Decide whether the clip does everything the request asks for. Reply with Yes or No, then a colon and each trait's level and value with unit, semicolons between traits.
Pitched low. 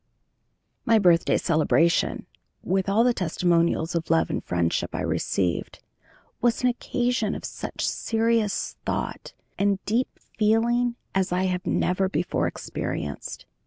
No: high, 190 Hz